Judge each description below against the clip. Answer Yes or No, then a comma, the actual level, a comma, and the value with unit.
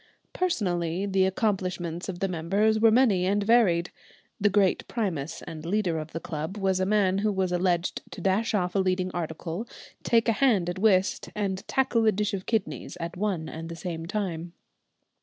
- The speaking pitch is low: No, high, 190 Hz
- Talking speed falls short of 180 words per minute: No, average, 185 wpm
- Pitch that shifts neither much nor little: Yes, average, 3.3 semitones